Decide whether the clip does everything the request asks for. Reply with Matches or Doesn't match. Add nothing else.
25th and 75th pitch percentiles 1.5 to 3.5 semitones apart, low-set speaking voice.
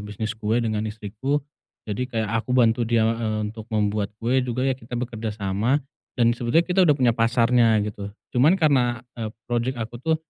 Matches